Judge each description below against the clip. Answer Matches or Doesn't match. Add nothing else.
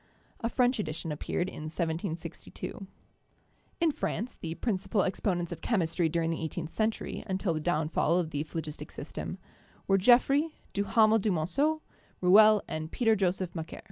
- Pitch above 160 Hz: Matches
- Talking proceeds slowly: Doesn't match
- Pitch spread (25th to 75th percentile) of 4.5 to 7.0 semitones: Matches